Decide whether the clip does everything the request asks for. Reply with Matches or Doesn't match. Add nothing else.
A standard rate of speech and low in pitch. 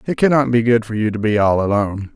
Doesn't match